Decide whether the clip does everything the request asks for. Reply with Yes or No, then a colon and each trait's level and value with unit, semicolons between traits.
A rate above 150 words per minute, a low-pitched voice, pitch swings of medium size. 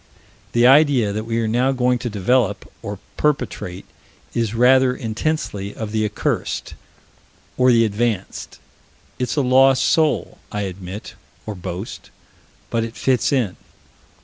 No: slow, 135 wpm; low, 115 Hz; average, 3.6 semitones